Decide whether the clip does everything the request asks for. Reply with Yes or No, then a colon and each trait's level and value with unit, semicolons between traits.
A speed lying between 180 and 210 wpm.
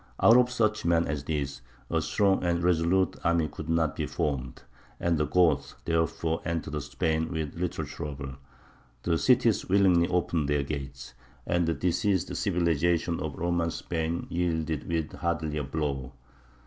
No: average, 150 wpm